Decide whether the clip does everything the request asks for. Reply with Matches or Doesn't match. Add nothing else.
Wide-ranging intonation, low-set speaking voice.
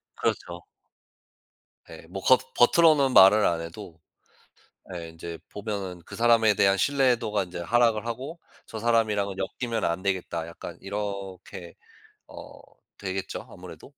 Doesn't match